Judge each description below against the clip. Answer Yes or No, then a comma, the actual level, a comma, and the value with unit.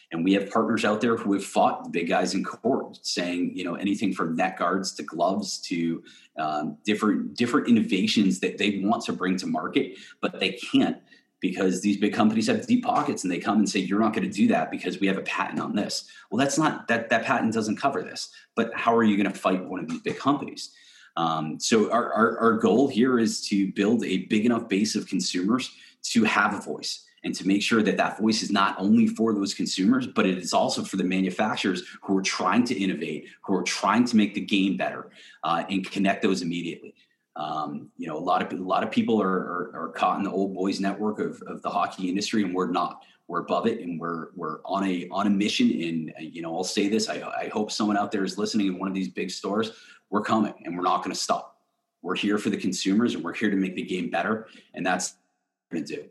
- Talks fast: Yes, fast, 245 wpm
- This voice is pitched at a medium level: No, low, 100 Hz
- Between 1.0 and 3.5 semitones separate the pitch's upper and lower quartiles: Yes, narrow, 2.4 semitones